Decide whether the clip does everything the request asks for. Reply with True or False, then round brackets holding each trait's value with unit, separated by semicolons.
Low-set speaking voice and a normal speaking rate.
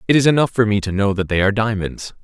False (105 Hz; 295 wpm)